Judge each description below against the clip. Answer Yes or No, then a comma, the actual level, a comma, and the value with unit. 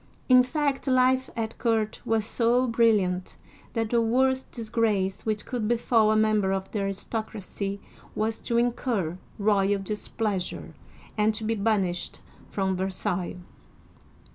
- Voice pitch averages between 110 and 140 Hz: No, high, 220 Hz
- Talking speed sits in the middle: No, slow, 130 wpm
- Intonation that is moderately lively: Yes, average, 3.0 semitones